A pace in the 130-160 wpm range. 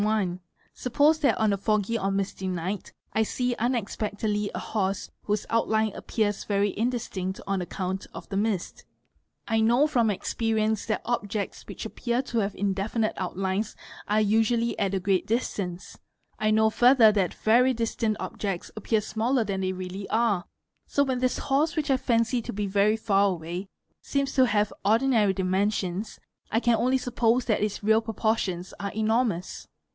No: average, 170 wpm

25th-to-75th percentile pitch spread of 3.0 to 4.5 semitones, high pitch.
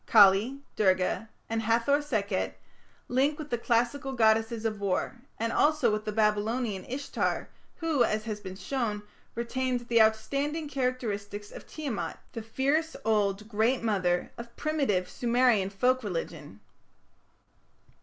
Yes: average, 3.8 semitones; high, 225 Hz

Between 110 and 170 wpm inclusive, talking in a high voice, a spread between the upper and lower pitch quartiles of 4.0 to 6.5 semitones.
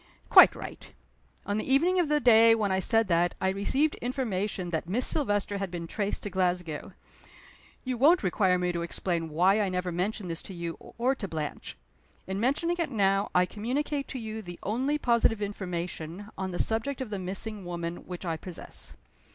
No: average, 190 wpm; high, 200 Hz; average, 4.7 semitones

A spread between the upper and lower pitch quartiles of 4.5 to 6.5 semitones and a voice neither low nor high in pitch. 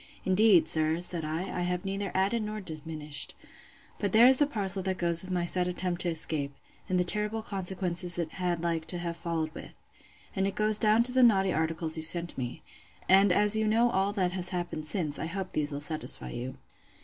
No: average, 3.4 semitones; medium, 180 Hz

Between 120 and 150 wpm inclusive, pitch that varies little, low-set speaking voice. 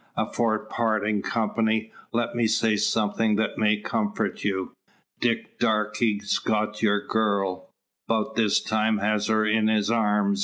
Yes: average, 140 wpm; narrow, 1.1 semitones; low, 110 Hz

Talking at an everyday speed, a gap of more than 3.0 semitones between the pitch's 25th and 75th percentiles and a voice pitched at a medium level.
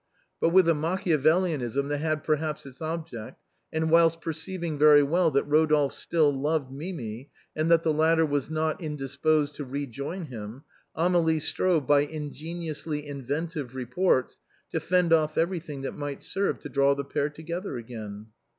No: average, 160 wpm; average, 2.7 semitones; medium, 155 Hz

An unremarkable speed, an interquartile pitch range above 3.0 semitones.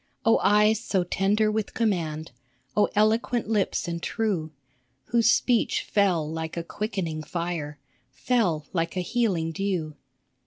No: slow, 130 wpm; average, 4.8 semitones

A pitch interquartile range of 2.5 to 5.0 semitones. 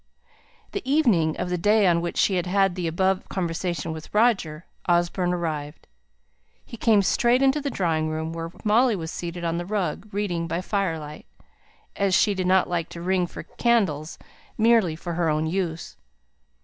Yes: average, 3.5 semitones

